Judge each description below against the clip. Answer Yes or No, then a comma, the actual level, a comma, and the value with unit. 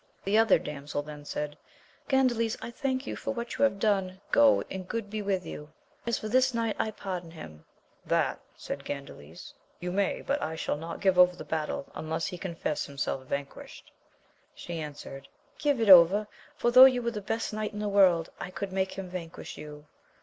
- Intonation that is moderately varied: No, wide, 5.9 semitones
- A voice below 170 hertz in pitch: No, high, 190 Hz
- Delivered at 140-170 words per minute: No, average, 195 wpm